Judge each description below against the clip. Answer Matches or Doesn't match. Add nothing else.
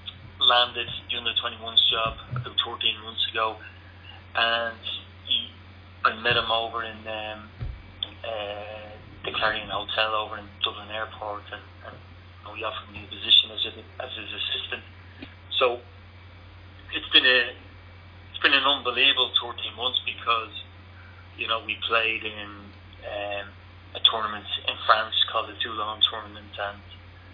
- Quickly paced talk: Doesn't match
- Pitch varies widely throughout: Doesn't match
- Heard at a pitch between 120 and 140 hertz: Doesn't match